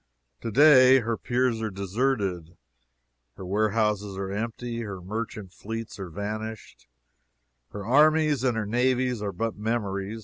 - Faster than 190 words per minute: No, slow, 135 wpm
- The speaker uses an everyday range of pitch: Yes, average, 3.4 semitones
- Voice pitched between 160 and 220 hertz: No, low, 110 Hz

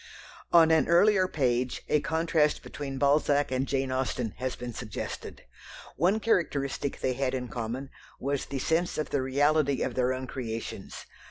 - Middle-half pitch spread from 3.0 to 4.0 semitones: Yes, average, 3.3 semitones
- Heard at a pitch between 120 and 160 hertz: Yes, medium, 140 Hz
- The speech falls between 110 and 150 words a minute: No, average, 160 wpm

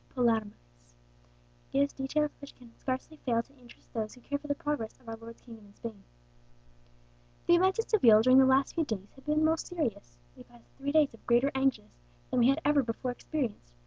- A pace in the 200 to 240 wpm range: Yes, fast, 205 wpm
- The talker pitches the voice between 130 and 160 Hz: No, very high, 255 Hz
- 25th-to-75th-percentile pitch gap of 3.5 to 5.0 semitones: Yes, average, 4.1 semitones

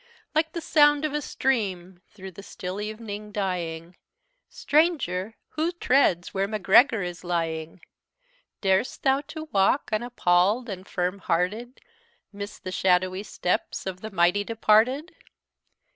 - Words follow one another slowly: Yes, slow, 130 wpm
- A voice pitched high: Yes, high, 200 Hz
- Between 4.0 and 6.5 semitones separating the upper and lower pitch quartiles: Yes, average, 5.3 semitones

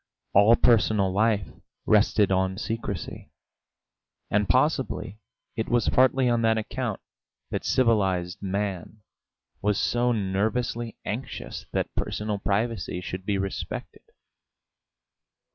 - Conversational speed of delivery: No, slow, 105 wpm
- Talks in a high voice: No, low, 105 Hz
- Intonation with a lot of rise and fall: No, average, 2.9 semitones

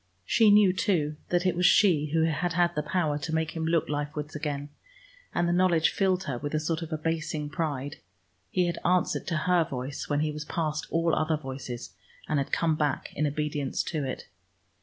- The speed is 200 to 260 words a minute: Yes, fast, 205 wpm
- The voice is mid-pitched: Yes, medium, 155 Hz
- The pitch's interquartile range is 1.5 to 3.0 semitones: Yes, average, 2.7 semitones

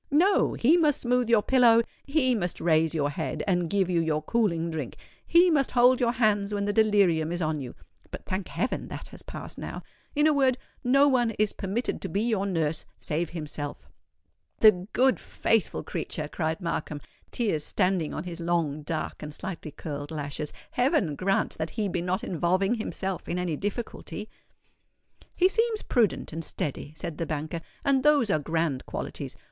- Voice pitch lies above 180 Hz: Yes, high, 190 Hz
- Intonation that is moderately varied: No, wide, 7.0 semitones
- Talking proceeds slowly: No, average, 170 wpm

